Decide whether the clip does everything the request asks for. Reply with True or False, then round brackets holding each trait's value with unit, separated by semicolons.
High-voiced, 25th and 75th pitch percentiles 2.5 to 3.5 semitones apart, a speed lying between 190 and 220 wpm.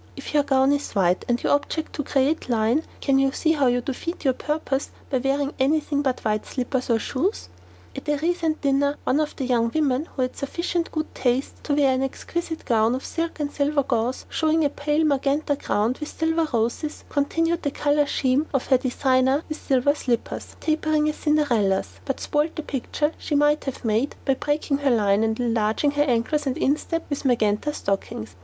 True (280 Hz; 3.2 semitones; 195 wpm)